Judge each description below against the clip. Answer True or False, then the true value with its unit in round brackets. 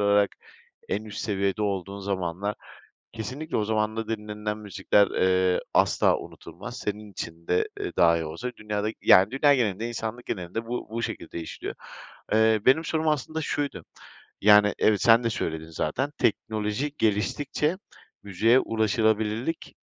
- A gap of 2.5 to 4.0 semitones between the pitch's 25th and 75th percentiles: True (2.8 semitones)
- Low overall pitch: True (105 Hz)